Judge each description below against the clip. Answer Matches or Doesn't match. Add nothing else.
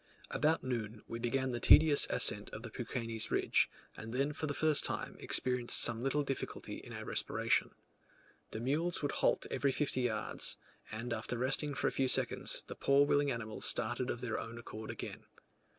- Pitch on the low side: Matches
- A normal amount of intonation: Matches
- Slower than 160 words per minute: Doesn't match